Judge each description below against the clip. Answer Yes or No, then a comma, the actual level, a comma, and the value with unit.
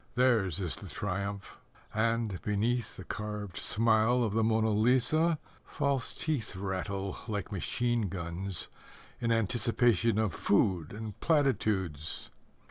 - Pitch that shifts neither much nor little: Yes, average, 3.3 semitones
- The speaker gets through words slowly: Yes, slow, 120 wpm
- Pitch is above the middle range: No, low, 110 Hz